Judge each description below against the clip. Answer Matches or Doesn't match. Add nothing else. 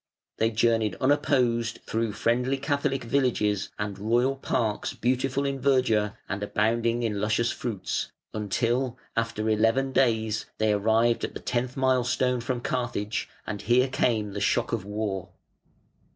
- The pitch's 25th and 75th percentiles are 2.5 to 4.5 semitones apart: Matches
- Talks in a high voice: Doesn't match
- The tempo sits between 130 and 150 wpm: Matches